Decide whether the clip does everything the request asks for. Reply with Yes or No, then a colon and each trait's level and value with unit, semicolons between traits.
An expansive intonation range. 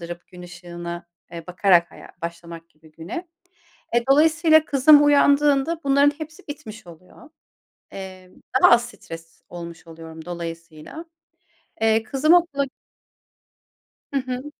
Yes: wide, 9.0 semitones